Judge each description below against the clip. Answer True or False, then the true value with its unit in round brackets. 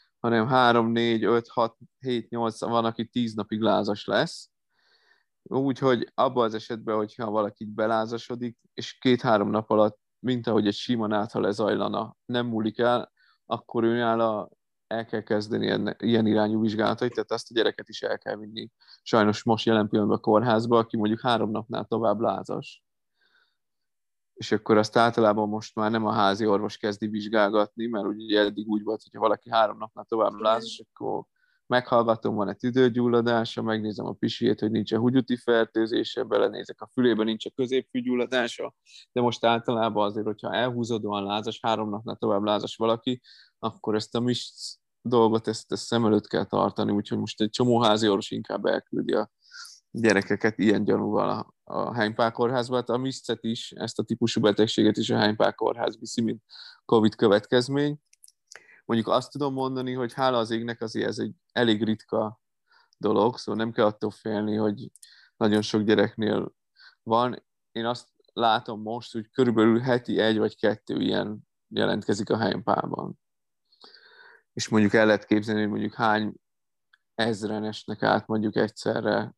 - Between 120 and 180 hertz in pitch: False (110 Hz)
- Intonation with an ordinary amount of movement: False (1.8 semitones)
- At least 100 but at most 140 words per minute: False (155 wpm)